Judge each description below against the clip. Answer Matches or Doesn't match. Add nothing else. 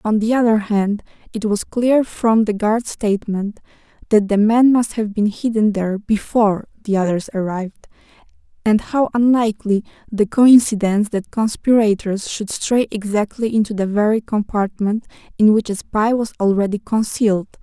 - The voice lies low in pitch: Doesn't match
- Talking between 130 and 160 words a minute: Matches